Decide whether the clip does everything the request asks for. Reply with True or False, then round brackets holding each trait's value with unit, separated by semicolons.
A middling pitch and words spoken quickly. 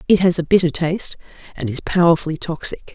False (165 Hz; 185 wpm)